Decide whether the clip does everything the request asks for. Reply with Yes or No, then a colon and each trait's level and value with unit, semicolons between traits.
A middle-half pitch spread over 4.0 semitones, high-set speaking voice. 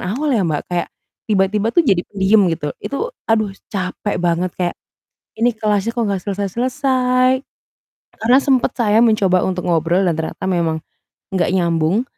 Yes: average, 4.5 semitones; high, 200 Hz